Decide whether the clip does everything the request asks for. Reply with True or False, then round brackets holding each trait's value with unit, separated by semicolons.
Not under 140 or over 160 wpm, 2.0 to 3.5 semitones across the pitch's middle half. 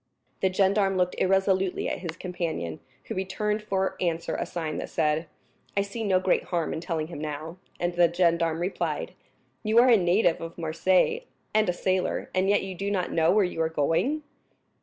False (190 wpm; 2.8 semitones)